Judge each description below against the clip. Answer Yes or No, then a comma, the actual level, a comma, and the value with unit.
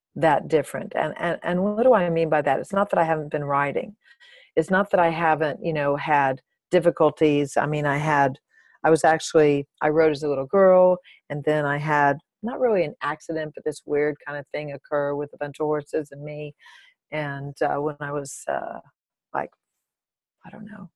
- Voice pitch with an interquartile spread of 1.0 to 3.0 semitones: Yes, average, 2.7 semitones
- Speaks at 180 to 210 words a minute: Yes, fast, 205 wpm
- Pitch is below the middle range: No, medium, 150 Hz